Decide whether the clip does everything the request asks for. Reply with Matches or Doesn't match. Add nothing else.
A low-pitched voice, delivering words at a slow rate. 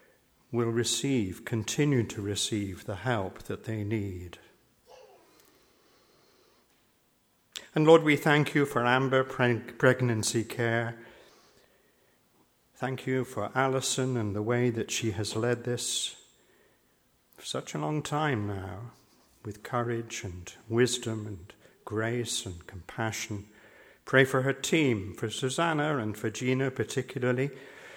Matches